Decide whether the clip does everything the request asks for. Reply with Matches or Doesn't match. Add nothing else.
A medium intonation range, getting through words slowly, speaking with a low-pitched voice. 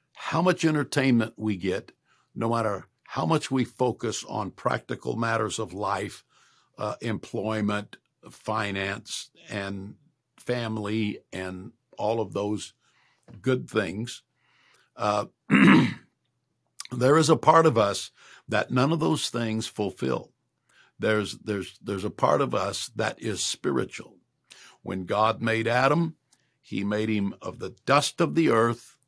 Matches